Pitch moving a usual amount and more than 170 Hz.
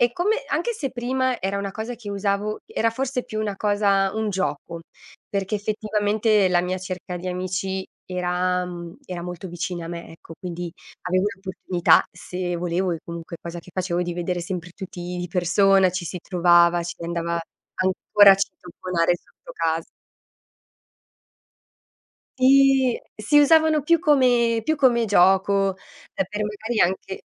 Yes: average, 3.5 semitones; high, 190 Hz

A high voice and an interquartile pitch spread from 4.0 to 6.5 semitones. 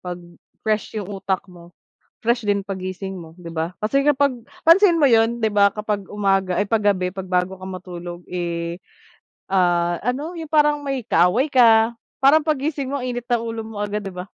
Yes: high, 205 Hz; wide, 5.5 semitones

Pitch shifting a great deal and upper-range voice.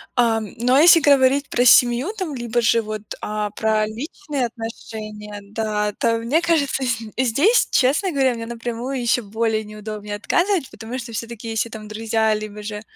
No: average, 3.3 semitones; high, 230 Hz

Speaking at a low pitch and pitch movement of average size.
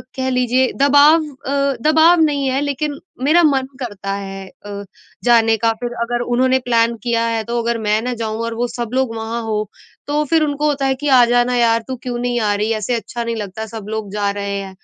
No: high, 240 Hz; average, 3.4 semitones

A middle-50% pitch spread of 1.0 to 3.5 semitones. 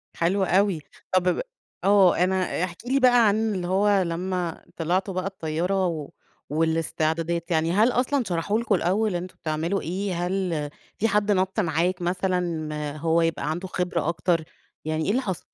Yes: average, 3.0 semitones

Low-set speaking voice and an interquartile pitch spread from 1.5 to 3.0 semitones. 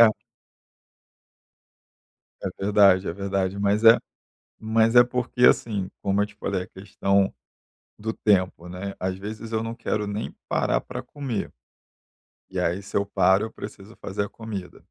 Yes: low, 100 Hz; narrow, 2.4 semitones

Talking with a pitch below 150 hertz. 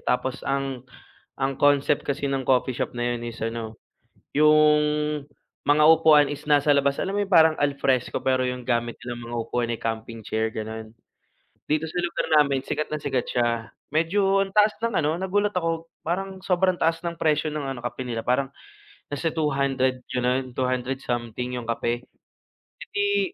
Yes: medium, 140 Hz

